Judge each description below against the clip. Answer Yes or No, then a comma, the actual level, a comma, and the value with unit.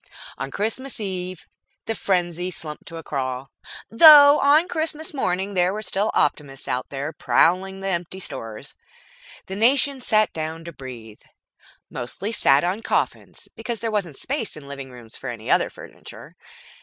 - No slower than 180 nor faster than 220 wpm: No, average, 160 wpm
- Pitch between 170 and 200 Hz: Yes, medium, 185 Hz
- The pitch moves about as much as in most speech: No, wide, 8.0 semitones